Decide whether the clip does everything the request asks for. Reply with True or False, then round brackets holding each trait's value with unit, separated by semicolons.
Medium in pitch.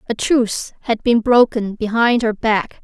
False (230 Hz)